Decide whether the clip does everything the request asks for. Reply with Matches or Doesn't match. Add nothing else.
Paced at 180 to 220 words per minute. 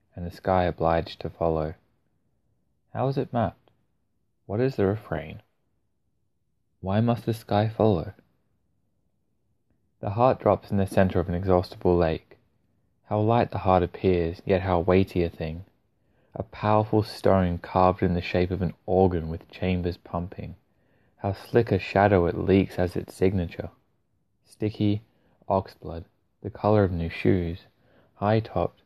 Doesn't match